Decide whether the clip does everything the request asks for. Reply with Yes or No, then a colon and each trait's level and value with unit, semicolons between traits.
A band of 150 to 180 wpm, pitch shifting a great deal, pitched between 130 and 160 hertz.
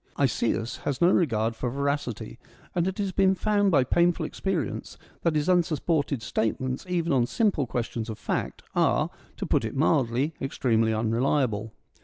Yes: average, 160 wpm; wide, 6.6 semitones; medium, 140 Hz